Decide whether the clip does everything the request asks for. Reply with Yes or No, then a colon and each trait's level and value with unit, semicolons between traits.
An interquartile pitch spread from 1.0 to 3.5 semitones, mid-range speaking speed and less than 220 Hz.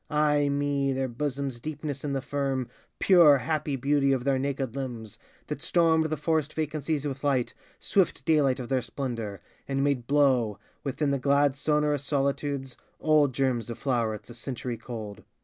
Yes: narrow, 2.4 semitones; average, 165 wpm; medium, 140 Hz